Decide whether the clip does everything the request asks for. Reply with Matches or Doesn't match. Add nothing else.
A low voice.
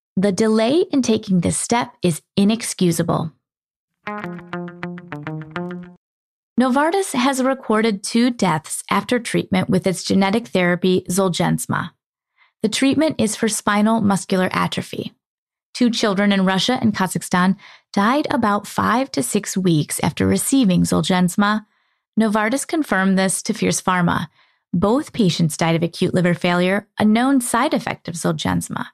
Doesn't match